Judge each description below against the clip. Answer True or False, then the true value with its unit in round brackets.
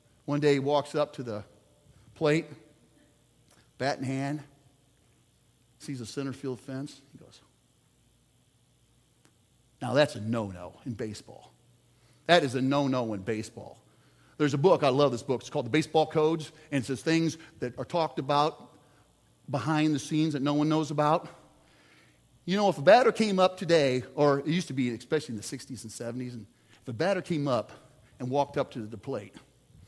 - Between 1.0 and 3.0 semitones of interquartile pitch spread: False (3.7 semitones)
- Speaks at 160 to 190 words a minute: True (180 wpm)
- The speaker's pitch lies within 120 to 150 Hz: True (140 Hz)